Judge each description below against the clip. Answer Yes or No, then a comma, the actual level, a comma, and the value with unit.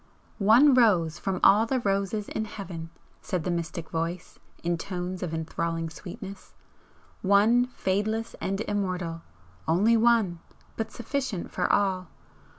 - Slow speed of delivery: Yes, slow, 130 wpm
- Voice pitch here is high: Yes, high, 195 Hz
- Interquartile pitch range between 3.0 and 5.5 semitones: Yes, average, 4.2 semitones